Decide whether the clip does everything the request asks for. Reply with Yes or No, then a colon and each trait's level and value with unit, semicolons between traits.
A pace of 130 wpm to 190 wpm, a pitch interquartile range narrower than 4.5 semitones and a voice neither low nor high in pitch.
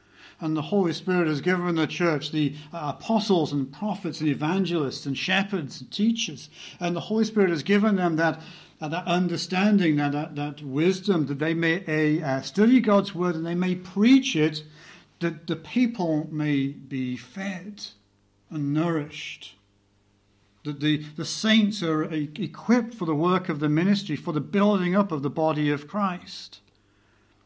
Yes: average, 165 wpm; average, 4.0 semitones; medium, 160 Hz